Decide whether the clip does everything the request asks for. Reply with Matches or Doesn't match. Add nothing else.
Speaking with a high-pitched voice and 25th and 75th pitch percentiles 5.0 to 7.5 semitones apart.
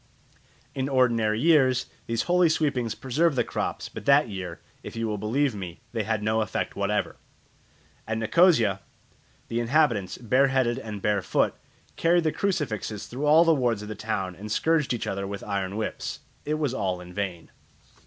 Doesn't match